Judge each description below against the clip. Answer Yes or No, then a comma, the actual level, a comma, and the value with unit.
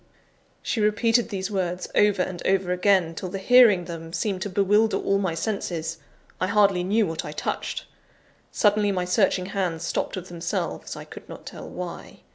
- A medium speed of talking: Yes, average, 175 wpm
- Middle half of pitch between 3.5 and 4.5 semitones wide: No, narrow, 2.6 semitones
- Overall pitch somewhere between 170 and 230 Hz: Yes, high, 190 Hz